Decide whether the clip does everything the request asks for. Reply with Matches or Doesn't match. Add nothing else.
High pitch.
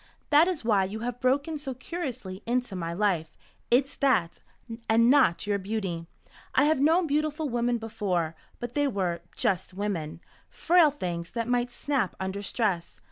Matches